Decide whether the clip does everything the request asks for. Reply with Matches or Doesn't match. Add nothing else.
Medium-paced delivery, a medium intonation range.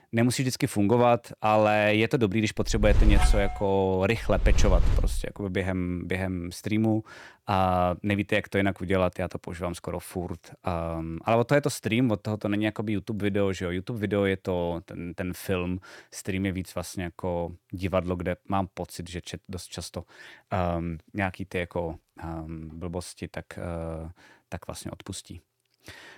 Doesn't match